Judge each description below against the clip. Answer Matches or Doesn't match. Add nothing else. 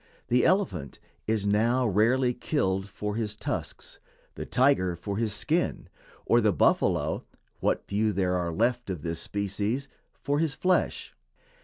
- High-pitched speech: Doesn't match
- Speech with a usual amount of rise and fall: Matches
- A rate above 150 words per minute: Doesn't match